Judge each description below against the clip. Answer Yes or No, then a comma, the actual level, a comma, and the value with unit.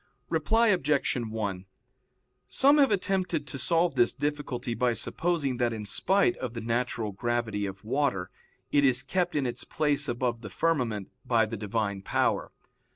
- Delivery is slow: No, average, 155 wpm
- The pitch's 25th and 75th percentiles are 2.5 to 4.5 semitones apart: No, average, 5.2 semitones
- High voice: No, low, 125 Hz